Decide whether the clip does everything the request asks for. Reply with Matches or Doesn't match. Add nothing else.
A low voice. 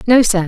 Doesn't match